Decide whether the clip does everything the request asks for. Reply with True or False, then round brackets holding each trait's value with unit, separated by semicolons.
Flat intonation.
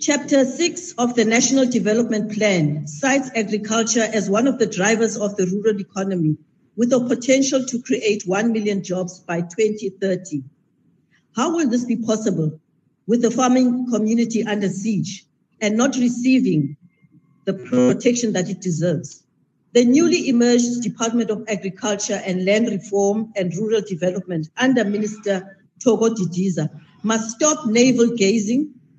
False (4.2 semitones)